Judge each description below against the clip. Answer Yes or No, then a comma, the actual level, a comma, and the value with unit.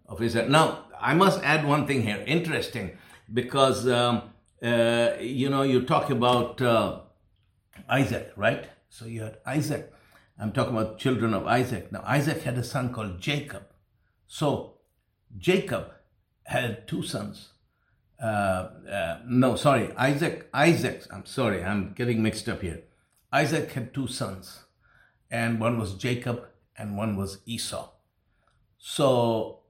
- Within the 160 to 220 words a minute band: No, slow, 135 wpm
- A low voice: Yes, low, 120 Hz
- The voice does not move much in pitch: No, average, 3.8 semitones